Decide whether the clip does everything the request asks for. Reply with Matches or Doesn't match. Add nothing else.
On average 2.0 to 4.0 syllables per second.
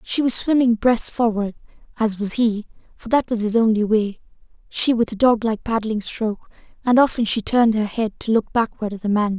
Doesn't match